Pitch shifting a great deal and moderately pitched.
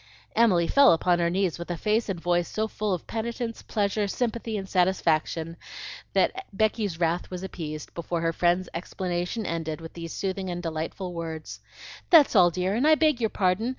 No: average, 4.2 semitones; medium, 180 Hz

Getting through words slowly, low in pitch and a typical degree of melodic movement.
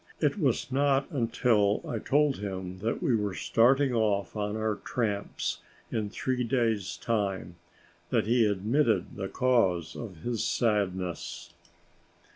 Yes: slow, 130 wpm; low, 110 Hz; average, 4.0 semitones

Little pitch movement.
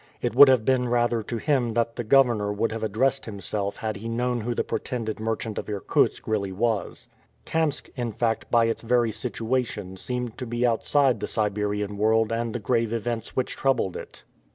Yes: narrow, 2.2 semitones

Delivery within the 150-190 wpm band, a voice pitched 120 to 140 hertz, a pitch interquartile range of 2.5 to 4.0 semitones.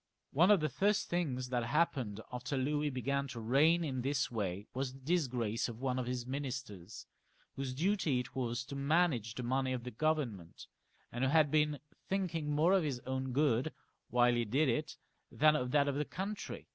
No: average, 200 wpm; low, 135 Hz; average, 3.7 semitones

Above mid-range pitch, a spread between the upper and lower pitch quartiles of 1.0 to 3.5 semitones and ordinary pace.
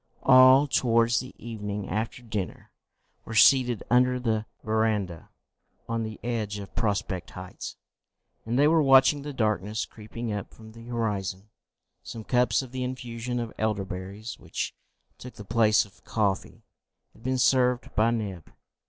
No: low, 115 Hz; average, 3.0 semitones; average, 150 wpm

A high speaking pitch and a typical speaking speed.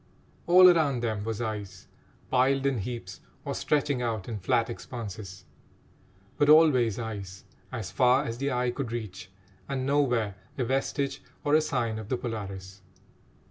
No: low, 120 Hz; average, 150 wpm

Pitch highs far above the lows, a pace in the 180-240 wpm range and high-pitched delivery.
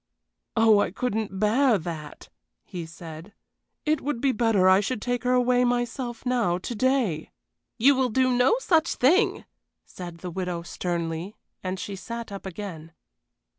No: wide, 5.7 semitones; average, 155 wpm; high, 215 Hz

